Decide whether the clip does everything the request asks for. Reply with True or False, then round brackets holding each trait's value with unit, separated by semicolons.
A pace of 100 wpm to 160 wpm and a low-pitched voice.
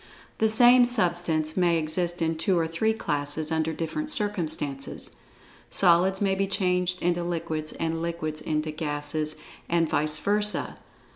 False (140 wpm; 170 Hz)